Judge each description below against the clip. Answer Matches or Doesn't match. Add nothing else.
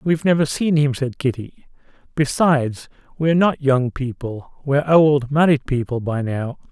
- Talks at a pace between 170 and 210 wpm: Doesn't match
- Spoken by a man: Matches